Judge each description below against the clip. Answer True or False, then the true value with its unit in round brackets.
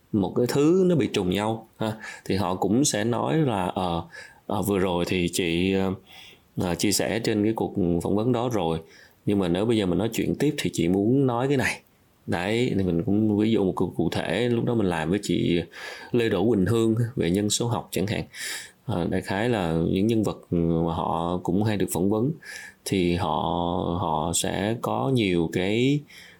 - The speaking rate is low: False (205 wpm)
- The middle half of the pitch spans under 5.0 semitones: True (4.4 semitones)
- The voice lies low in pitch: True (100 Hz)